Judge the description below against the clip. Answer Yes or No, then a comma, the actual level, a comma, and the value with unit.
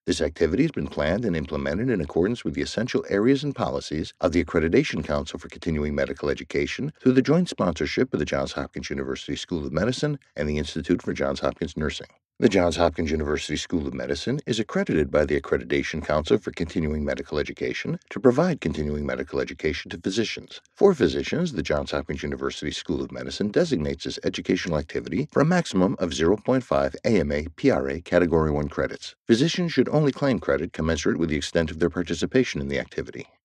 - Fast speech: No, average, 185 wpm